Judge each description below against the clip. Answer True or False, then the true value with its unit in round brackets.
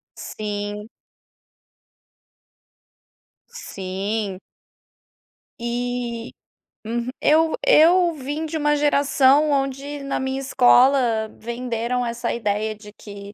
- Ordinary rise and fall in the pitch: True (4.5 semitones)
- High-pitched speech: True (245 Hz)